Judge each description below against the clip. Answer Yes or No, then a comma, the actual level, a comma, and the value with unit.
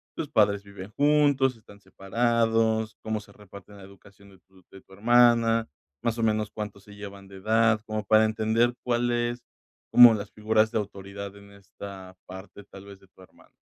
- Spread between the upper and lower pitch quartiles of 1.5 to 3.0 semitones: Yes, narrow, 2.4 semitones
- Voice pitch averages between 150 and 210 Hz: No, low, 105 Hz